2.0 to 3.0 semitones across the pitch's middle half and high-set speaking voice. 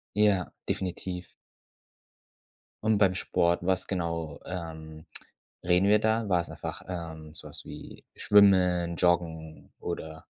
No: narrow, 2.5 semitones; very low, 90 Hz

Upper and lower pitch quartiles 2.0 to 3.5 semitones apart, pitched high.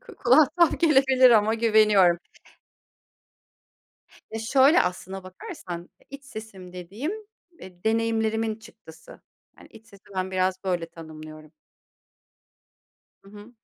No: average, 4.3 semitones; high, 215 Hz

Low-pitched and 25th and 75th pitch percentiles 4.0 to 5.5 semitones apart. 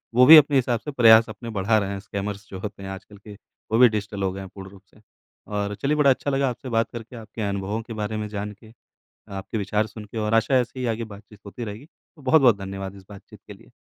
No: low, 105 Hz; average, 3.2 semitones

